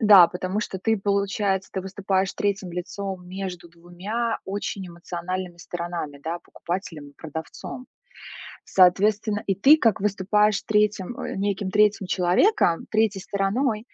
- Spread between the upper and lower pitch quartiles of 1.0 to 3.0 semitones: Yes, average, 2.7 semitones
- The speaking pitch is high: Yes, high, 195 Hz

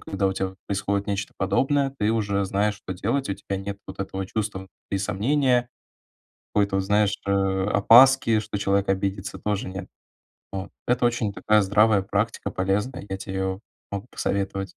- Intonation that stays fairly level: Yes, narrow, 1.7 semitones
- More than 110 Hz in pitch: No, low, 100 Hz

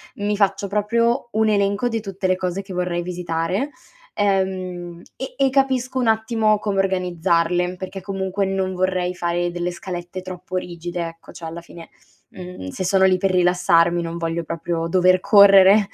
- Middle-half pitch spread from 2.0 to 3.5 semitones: Yes, narrow, 2.4 semitones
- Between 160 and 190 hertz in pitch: Yes, medium, 185 Hz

